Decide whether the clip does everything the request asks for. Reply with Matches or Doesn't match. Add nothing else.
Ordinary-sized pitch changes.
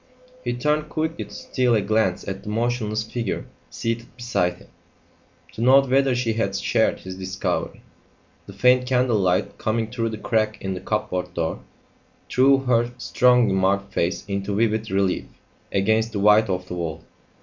Matches